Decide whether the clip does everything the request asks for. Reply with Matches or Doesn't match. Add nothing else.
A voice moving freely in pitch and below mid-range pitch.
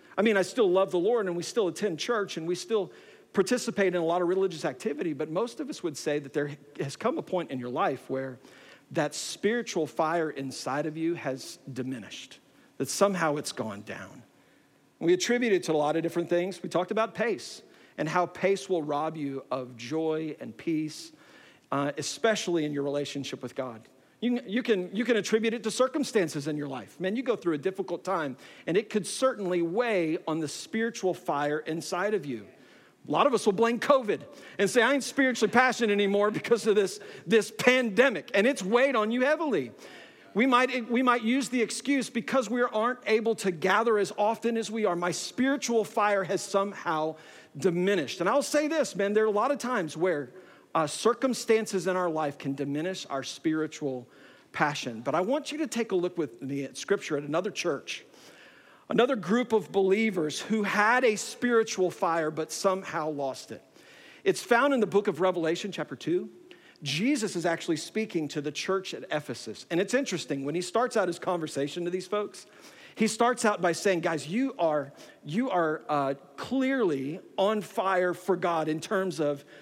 Doesn't match